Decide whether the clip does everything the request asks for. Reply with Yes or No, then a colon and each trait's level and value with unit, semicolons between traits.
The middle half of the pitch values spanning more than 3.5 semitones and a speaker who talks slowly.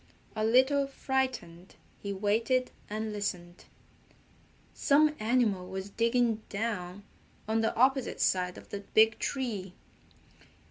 Yes: average, 4.3 semitones; slow, 110 wpm